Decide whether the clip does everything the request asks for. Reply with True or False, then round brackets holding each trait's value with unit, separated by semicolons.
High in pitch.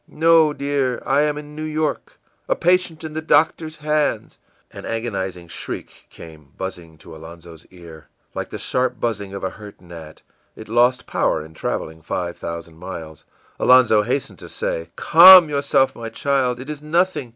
False (120 Hz)